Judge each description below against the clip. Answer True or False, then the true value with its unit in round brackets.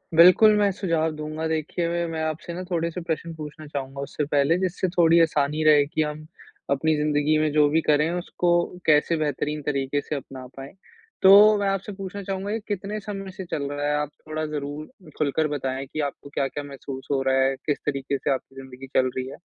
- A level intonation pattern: False (3.2 semitones)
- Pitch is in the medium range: True (155 Hz)